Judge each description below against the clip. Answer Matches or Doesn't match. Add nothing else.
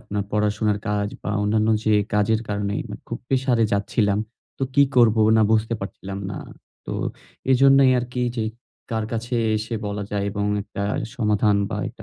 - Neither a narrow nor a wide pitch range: Doesn't match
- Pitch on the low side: Matches